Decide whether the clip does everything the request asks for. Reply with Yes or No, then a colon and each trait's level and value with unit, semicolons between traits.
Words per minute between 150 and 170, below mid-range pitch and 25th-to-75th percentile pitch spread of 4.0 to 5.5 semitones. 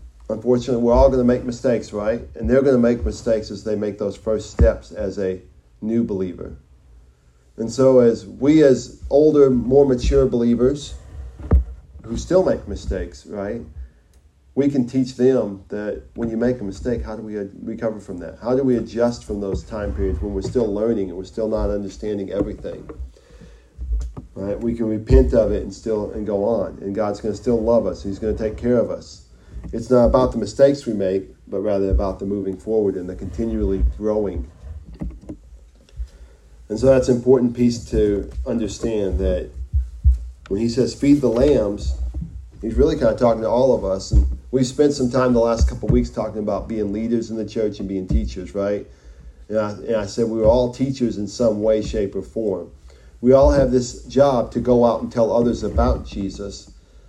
No: average, 195 wpm; low, 105 Hz; average, 4.6 semitones